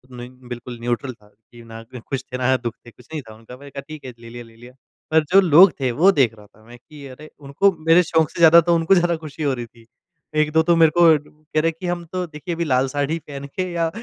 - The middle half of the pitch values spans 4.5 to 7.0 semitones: Yes, average, 5.2 semitones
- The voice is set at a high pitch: No, medium, 140 Hz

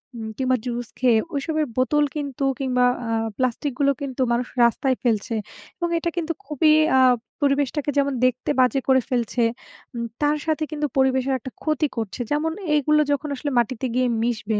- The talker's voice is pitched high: Yes, very high, 265 Hz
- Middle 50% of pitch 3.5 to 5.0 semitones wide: No, average, 3.1 semitones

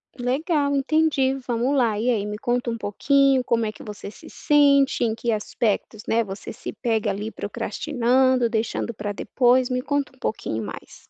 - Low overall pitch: No, high, 245 Hz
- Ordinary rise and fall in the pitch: Yes, average, 3.8 semitones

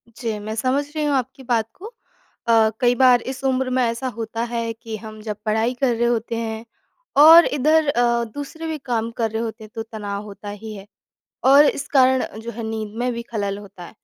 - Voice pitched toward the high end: Yes, high, 235 Hz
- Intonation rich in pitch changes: No, average, 3.0 semitones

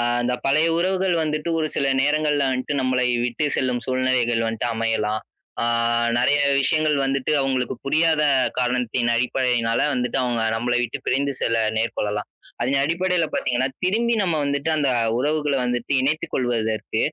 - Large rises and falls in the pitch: No, average, 3.9 semitones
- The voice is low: Yes, low, 130 Hz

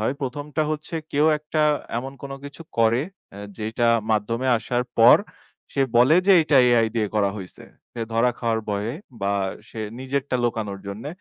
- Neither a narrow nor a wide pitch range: Yes, average, 4.0 semitones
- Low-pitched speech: Yes, low, 120 Hz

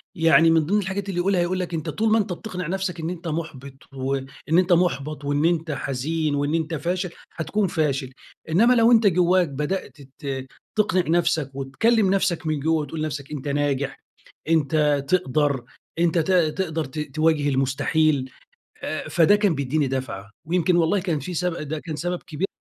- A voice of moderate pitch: Yes, medium, 160 Hz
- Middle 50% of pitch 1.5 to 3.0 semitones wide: No, average, 4.0 semitones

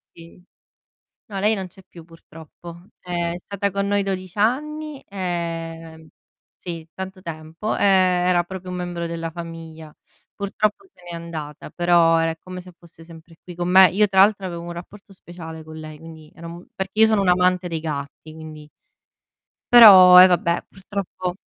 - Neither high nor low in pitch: Yes, medium, 175 Hz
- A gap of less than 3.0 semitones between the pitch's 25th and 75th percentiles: Yes, narrow, 2.5 semitones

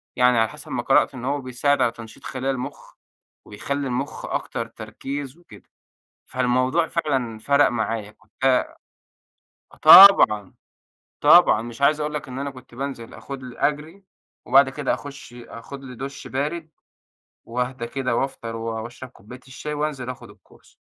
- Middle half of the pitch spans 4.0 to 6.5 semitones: No, average, 3.2 semitones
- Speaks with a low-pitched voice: Yes, low, 130 Hz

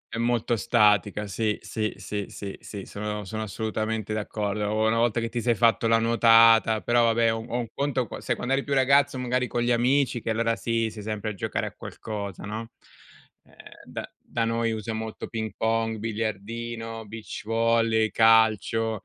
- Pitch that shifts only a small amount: Yes, narrow, 1.4 semitones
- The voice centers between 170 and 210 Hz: No, low, 115 Hz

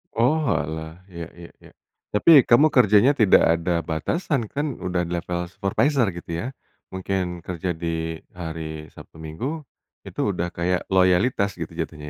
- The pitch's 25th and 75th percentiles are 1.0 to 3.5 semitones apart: No, wide, 5.5 semitones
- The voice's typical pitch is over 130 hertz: No, very low, 90 Hz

